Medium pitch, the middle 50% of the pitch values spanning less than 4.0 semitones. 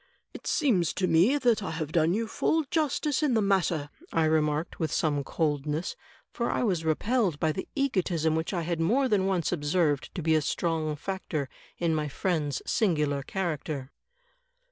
No: medium, 165 Hz; average, 4.3 semitones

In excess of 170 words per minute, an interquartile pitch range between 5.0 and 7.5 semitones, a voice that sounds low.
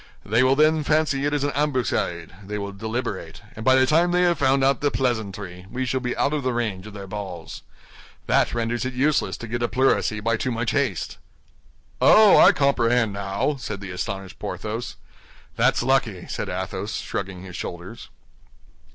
Yes: average, 185 wpm; average, 5.3 semitones; low, 120 Hz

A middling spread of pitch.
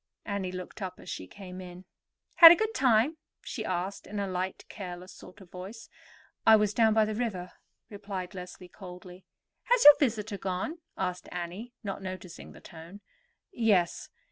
Yes: average, 3.2 semitones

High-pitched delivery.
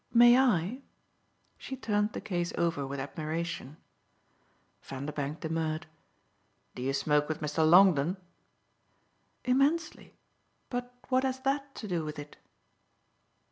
No: medium, 170 Hz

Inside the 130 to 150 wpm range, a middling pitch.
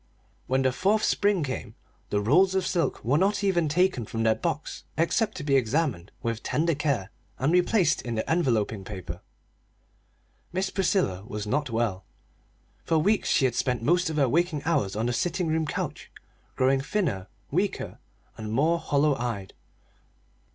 No: average, 165 wpm; medium, 145 Hz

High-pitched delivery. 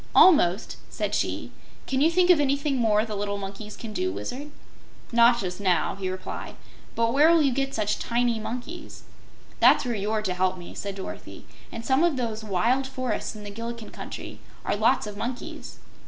Yes: high, 230 Hz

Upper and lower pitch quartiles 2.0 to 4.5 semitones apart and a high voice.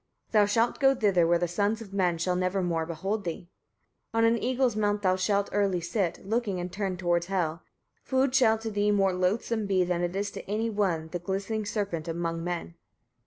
Yes: average, 3.4 semitones; high, 195 Hz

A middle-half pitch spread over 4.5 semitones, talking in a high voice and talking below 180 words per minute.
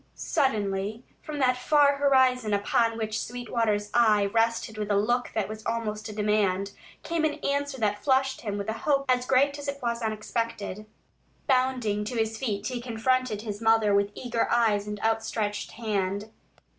No: average, 3.3 semitones; high, 225 Hz; average, 170 wpm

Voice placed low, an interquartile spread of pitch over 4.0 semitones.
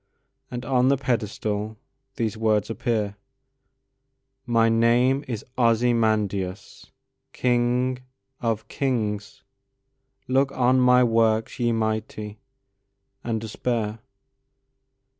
No: low, 115 Hz; average, 2.7 semitones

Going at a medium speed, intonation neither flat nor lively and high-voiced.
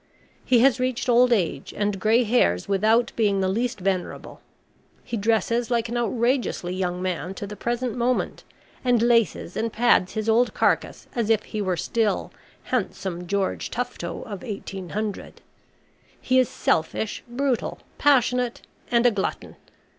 Yes: average, 145 wpm; average, 3.8 semitones; high, 225 Hz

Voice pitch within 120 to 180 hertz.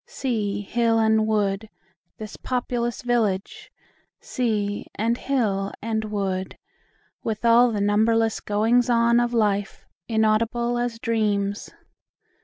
No: high, 220 Hz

